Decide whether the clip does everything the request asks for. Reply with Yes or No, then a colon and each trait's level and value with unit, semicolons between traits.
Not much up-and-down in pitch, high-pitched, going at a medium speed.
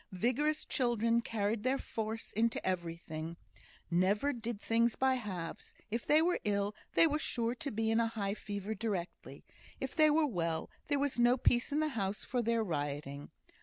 No: average, 4.4 semitones; high, 225 Hz; average, 175 wpm